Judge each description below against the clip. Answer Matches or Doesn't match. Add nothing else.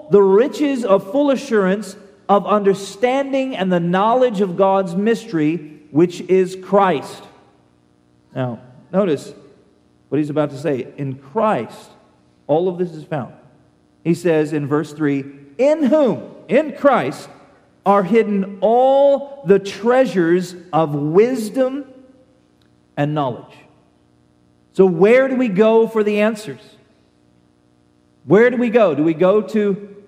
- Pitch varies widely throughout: Matches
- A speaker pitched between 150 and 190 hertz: Matches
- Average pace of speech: Doesn't match